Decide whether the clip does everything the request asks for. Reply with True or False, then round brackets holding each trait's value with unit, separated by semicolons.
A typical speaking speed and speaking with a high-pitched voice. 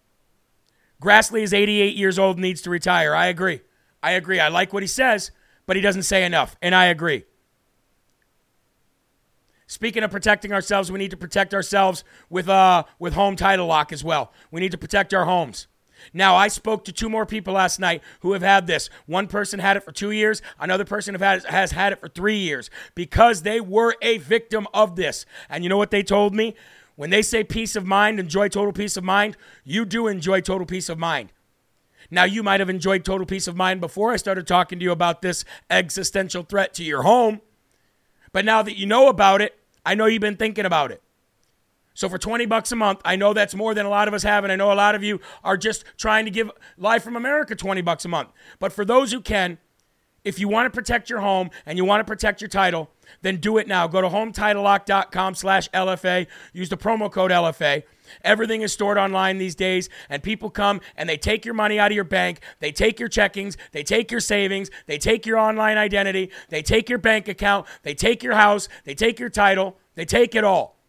False (225 wpm; 195 Hz)